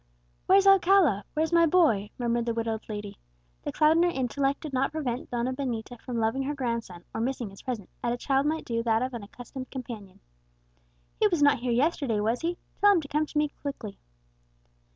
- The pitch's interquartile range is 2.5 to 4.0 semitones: No, average, 4.7 semitones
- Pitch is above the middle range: Yes, very high, 255 Hz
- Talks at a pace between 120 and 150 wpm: No, fast, 205 wpm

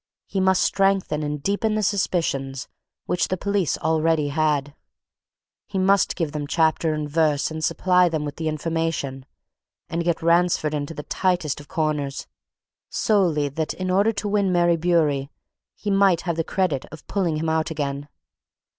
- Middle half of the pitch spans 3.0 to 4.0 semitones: Yes, average, 3.7 semitones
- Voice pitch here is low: No, medium, 165 Hz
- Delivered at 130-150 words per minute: No, average, 160 wpm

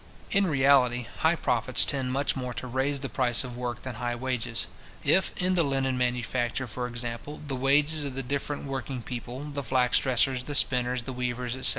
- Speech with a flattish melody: Yes, narrow, 2.2 semitones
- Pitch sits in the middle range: No, low, 130 Hz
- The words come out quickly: No, average, 195 wpm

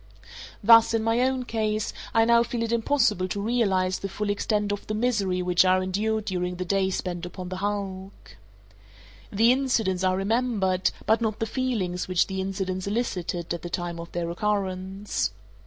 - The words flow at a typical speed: Yes, average, 175 wpm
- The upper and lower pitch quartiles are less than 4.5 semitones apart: Yes, average, 3.3 semitones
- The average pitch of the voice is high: Yes, high, 200 Hz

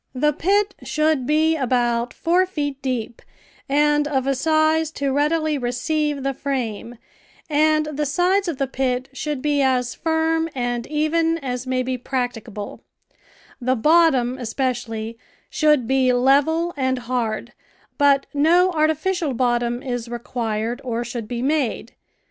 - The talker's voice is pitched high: Yes, very high, 270 Hz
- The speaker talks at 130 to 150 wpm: Yes, slow, 135 wpm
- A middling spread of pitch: Yes, average, 4.0 semitones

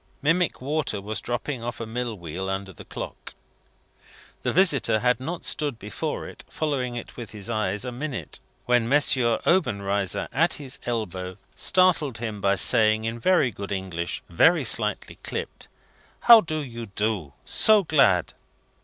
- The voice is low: Yes, low, 115 Hz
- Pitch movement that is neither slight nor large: No, wide, 6.2 semitones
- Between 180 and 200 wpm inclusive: No, average, 155 wpm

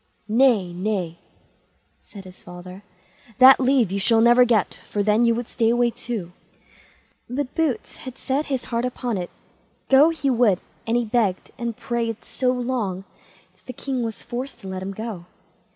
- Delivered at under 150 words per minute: No, average, 170 wpm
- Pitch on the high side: Yes, high, 235 Hz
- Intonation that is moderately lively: Yes, average, 4.2 semitones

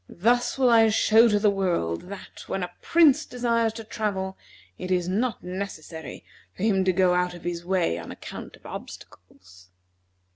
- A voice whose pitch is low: No, high, 190 Hz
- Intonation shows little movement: No, average, 4.2 semitones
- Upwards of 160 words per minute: Yes, average, 175 wpm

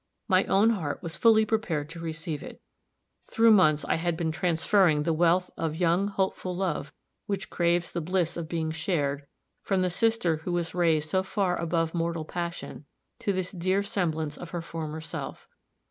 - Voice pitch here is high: No, medium, 170 Hz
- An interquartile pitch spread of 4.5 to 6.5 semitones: No, average, 2.8 semitones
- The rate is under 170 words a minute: No, average, 175 wpm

